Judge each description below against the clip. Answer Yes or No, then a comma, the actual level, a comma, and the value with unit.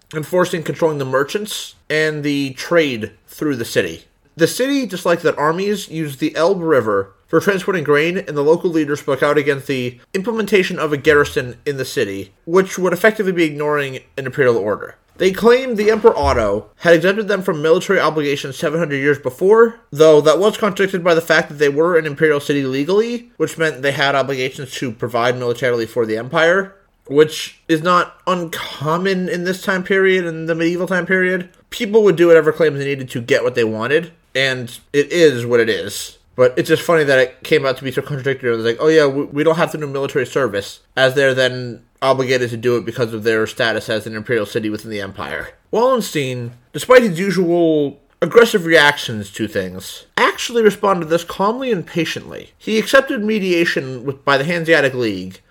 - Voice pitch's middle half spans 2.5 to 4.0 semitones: No, wide, 5.6 semitones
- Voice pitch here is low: No, medium, 155 Hz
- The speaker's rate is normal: Yes, average, 195 wpm